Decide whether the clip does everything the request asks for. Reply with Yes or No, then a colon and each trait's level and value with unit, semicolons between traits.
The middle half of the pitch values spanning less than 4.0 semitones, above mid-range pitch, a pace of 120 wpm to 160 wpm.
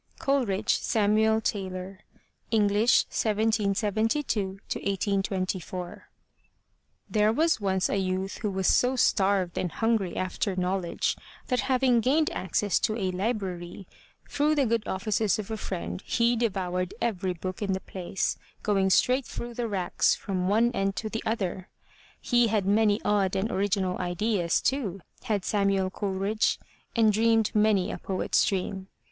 Yes: average, 2.9 semitones; high, 200 Hz; average, 140 wpm